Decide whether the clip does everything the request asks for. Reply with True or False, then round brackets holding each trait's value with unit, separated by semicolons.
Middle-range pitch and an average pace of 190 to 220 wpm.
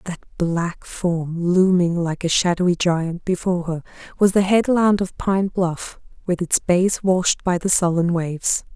False (180 Hz; 165 wpm)